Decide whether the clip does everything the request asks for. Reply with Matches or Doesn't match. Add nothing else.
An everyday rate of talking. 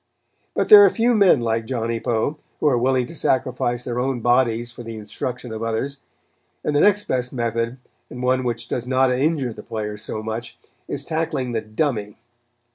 Matches